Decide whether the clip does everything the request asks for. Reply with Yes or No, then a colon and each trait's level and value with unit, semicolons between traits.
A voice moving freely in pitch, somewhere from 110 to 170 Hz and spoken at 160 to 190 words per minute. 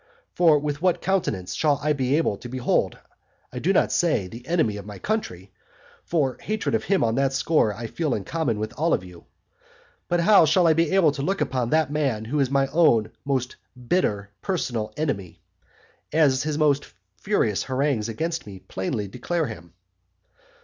Yes: wide, 6.6 semitones; medium, 140 Hz; average, 180 wpm